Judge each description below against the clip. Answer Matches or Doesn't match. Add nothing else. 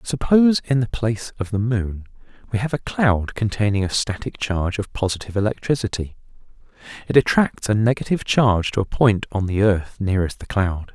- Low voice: Matches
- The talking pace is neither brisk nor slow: Matches